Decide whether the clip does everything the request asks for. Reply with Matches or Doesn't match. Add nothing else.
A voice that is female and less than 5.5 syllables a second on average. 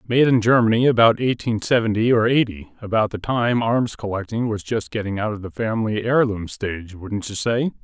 Doesn't match